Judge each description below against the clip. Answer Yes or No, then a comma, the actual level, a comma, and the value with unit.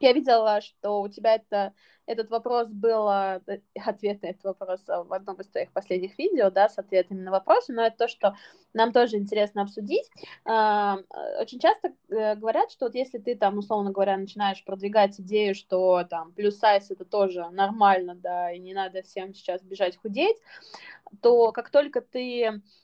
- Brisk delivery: Yes, fast, 170 wpm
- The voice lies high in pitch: Yes, high, 205 Hz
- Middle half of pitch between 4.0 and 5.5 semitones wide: No, average, 3.0 semitones